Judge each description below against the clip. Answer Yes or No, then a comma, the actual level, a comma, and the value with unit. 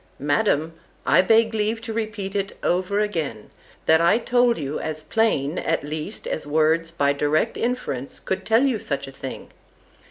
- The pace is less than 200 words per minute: Yes, average, 165 wpm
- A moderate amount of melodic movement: No, wide, 6.9 semitones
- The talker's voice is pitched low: No, medium, 170 Hz